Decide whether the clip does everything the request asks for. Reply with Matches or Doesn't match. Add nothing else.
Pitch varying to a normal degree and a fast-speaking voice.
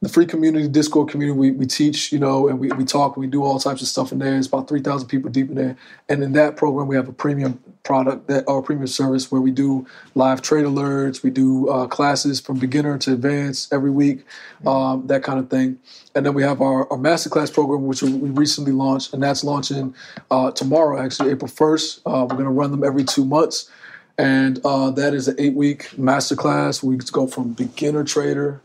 Doesn't match